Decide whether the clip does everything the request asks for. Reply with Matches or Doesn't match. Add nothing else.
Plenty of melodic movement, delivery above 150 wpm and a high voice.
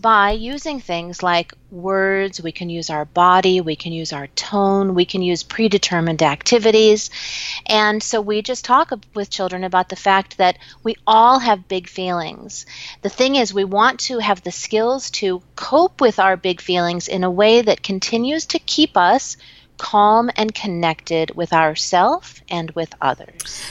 Doesn't match